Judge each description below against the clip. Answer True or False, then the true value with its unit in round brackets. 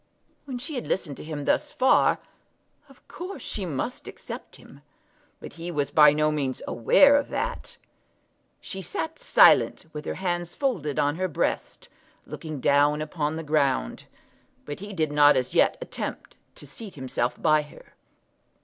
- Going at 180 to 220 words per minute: False (160 wpm)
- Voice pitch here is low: False (155 Hz)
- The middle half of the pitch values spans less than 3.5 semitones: False (4.7 semitones)